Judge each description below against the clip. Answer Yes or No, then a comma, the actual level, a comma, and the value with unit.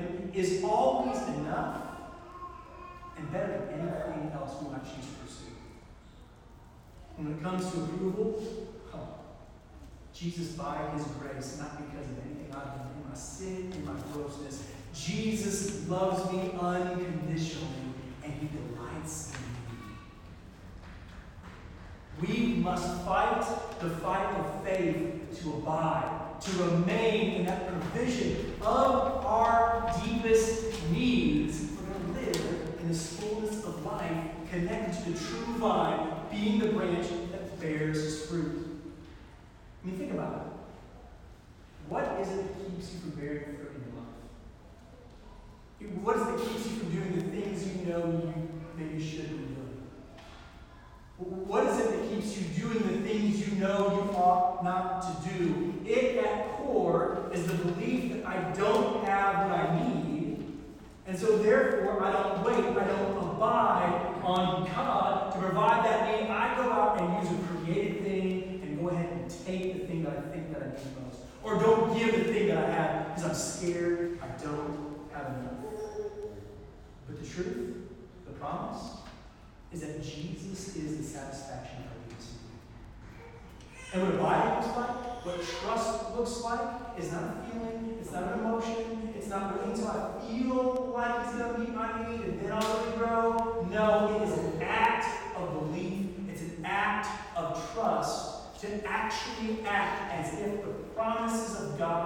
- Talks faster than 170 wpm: No, average, 155 wpm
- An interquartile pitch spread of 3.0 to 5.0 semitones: No, wide, 5.5 semitones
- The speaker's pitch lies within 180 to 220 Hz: Yes, medium, 185 Hz